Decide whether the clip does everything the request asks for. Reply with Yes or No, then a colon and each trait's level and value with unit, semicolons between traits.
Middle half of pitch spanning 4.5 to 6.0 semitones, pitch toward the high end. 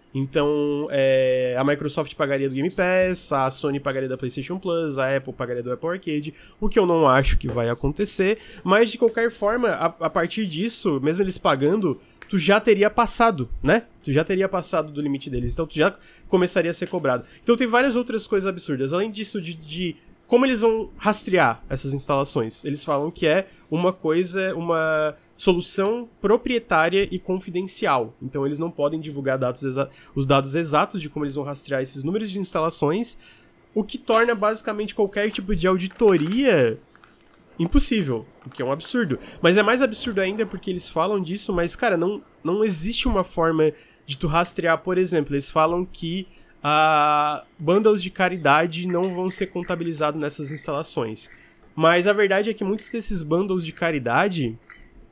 No: wide, 5.5 semitones; medium, 175 Hz